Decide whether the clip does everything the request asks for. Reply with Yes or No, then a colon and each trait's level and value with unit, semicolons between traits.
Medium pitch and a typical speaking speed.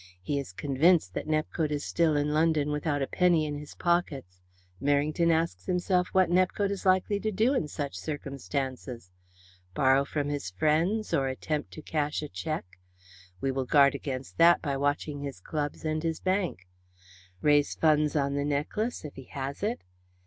Yes: medium, 150 Hz; average, 170 wpm